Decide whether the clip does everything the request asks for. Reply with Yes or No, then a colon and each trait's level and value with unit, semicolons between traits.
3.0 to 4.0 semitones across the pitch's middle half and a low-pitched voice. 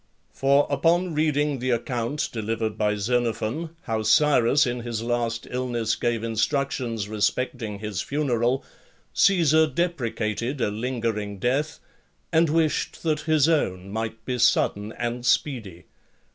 No: average, 4.7 semitones; low, 120 Hz